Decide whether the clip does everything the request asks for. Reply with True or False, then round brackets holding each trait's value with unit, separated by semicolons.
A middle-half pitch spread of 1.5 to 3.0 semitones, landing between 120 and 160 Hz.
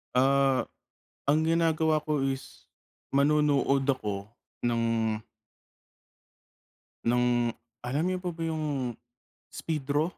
False (4.2 semitones; 140 Hz)